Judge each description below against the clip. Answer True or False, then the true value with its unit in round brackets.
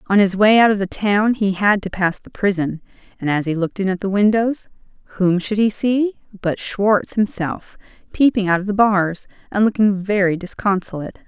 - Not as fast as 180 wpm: False (195 wpm)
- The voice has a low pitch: False (200 Hz)